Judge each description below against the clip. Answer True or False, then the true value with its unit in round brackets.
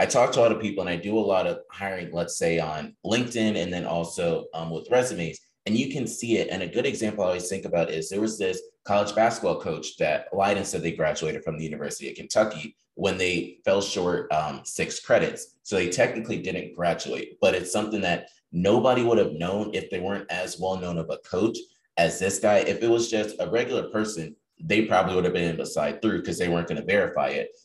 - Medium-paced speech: False (230 wpm)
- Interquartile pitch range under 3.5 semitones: False (4.5 semitones)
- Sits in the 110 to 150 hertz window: False (95 Hz)